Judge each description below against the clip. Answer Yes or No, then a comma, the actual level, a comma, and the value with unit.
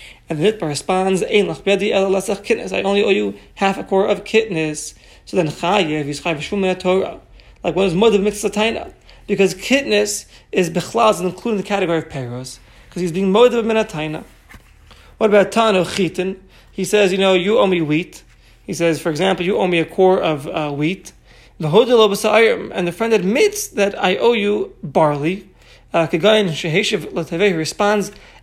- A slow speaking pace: No, average, 160 wpm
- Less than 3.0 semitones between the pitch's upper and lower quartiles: No, average, 3.6 semitones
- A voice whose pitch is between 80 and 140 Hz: No, high, 190 Hz